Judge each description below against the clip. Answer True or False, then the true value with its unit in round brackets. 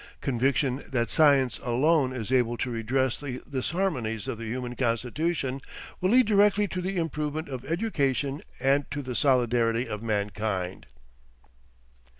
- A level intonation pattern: False (4.3 semitones)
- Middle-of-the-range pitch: False (130 Hz)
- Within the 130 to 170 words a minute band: True (140 wpm)